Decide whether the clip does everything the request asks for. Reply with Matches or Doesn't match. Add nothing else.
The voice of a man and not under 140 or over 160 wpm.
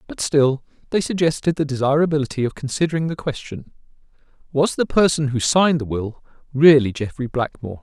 Matches